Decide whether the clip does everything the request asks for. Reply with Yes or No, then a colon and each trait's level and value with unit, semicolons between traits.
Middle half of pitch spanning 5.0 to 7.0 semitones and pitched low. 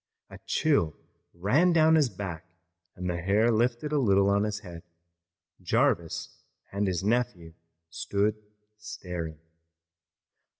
Yes: average, 5.3 semitones; low, 100 Hz